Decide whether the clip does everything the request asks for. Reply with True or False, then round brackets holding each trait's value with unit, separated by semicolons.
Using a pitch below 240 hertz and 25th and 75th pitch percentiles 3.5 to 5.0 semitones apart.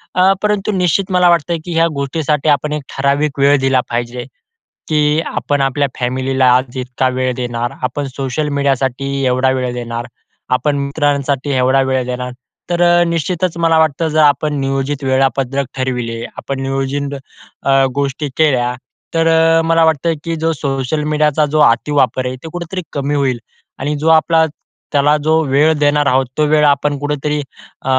False (140 Hz; 3.0 semitones)